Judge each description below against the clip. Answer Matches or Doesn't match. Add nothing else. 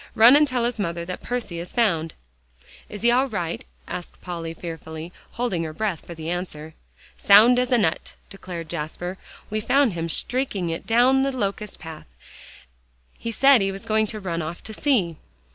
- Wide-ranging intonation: Matches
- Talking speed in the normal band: Matches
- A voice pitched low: Doesn't match